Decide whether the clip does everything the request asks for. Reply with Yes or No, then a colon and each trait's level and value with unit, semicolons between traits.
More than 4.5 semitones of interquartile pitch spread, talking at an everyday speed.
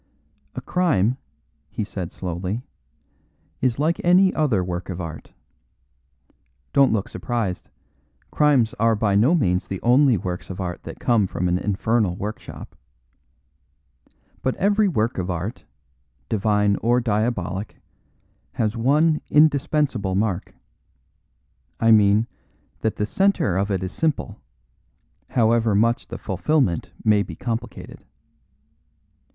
No: average, 5.2 semitones; slow, 120 wpm